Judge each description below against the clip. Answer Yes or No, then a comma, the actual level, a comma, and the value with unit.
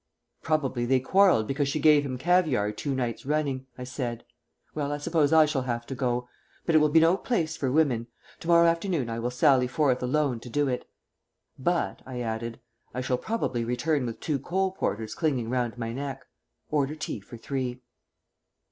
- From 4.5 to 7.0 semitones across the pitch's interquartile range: No, average, 4.0 semitones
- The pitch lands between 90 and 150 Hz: Yes, low, 135 Hz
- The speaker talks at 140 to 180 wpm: No, average, 190 wpm